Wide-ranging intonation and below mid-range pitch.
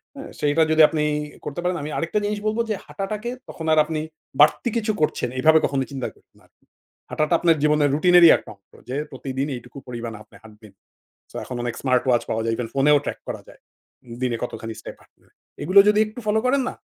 No: wide, 6.3 semitones; medium, 150 Hz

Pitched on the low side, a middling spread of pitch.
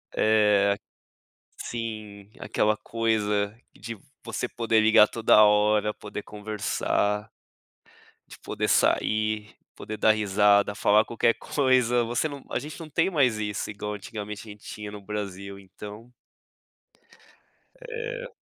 No: low, 105 Hz; narrow, 1.9 semitones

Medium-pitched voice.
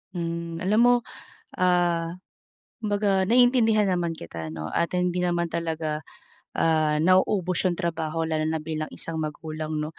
Yes: medium, 170 Hz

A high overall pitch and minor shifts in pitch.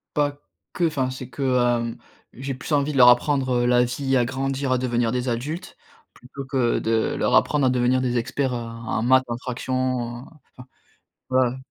No: low, 130 Hz; narrow, 1.6 semitones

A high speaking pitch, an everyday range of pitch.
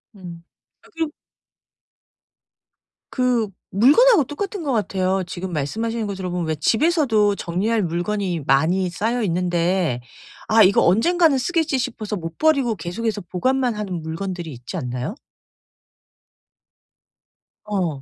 No: high, 200 Hz; wide, 5.8 semitones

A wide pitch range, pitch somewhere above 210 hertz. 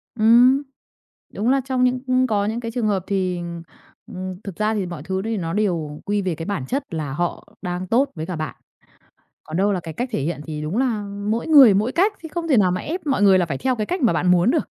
No: wide, 5.9 semitones; high, 205 Hz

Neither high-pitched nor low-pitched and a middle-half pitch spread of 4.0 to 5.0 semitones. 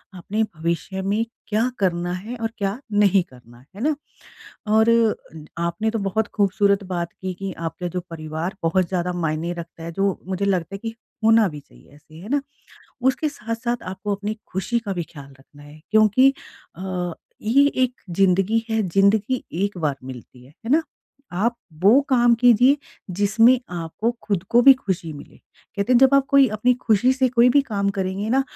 No: high, 200 Hz; average, 4.6 semitones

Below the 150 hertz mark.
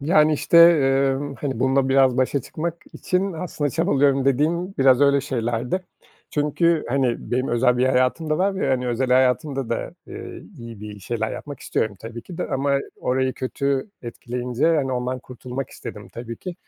Yes: low, 135 Hz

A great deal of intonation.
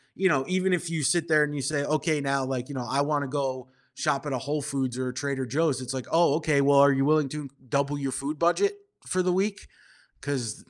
No: narrow, 2.6 semitones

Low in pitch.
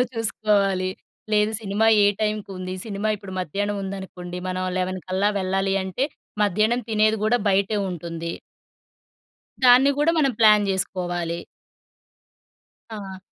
No: high, 195 Hz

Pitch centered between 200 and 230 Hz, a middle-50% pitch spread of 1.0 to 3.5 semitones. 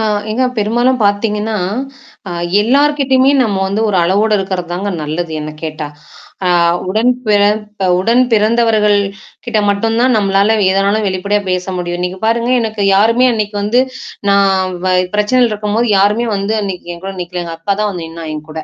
Yes: high, 205 Hz; average, 3.0 semitones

